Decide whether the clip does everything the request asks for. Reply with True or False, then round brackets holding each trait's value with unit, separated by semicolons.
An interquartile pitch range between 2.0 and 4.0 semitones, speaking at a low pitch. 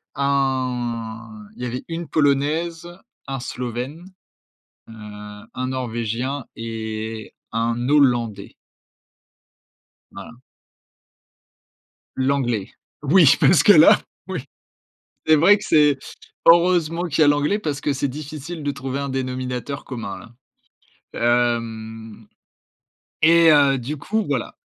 False (4.4 semitones; 130 Hz)